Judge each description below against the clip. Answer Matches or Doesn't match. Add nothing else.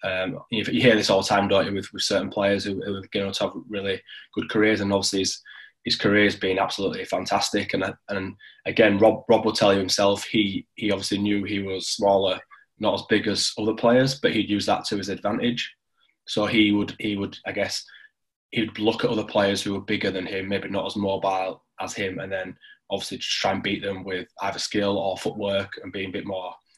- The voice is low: Matches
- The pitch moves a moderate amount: Doesn't match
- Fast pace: Matches